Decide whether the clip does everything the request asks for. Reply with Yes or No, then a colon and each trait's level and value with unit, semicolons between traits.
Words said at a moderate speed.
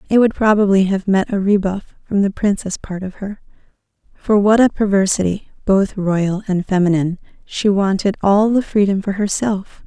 Yes: average, 170 wpm